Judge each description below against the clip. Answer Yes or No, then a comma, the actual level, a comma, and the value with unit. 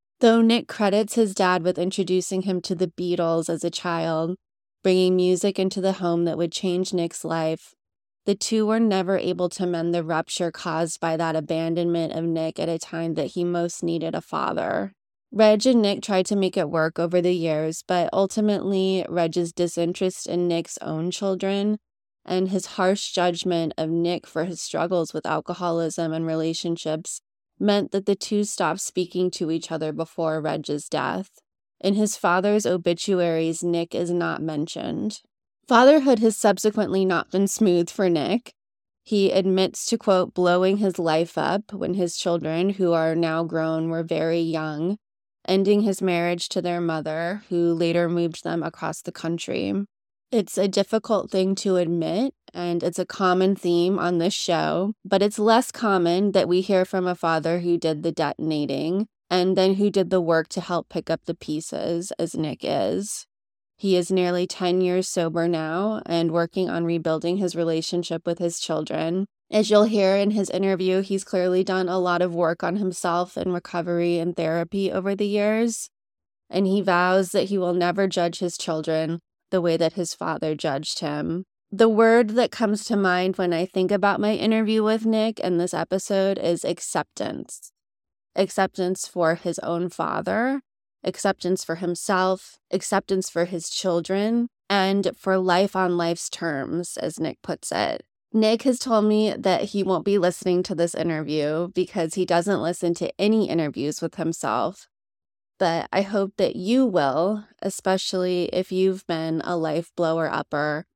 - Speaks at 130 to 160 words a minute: No, average, 170 wpm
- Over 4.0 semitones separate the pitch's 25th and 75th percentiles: No, narrow, 2.6 semitones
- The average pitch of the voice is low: No, medium, 180 Hz